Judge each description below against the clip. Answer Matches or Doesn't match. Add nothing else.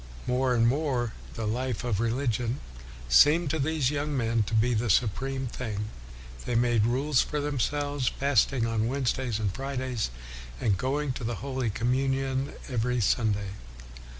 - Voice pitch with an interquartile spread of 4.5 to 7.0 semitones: Doesn't match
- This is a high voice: Doesn't match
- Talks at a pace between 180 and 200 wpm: Doesn't match